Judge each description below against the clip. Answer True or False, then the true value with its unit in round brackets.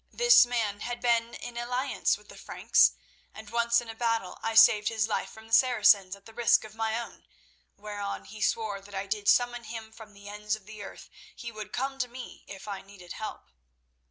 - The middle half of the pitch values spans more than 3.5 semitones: False (2.4 semitones)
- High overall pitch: True (220 Hz)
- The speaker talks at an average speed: False (215 wpm)